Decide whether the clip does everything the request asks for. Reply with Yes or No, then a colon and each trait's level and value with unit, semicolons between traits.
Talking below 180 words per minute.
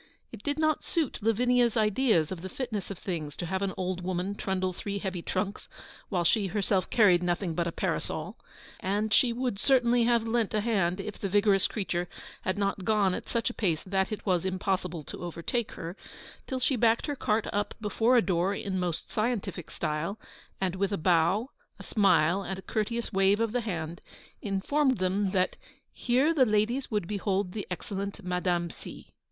No: average, 190 wpm